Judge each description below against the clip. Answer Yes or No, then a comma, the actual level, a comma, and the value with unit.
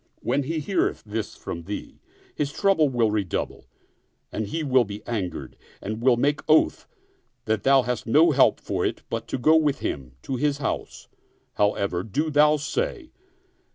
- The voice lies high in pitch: No, low, 130 Hz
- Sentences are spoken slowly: No, average, 165 wpm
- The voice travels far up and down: Yes, wide, 5.7 semitones